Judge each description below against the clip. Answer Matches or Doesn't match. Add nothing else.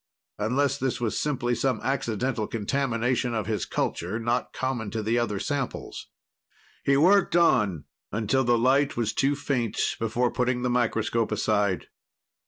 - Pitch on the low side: Matches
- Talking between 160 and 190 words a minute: Doesn't match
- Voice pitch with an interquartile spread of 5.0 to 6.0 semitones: Doesn't match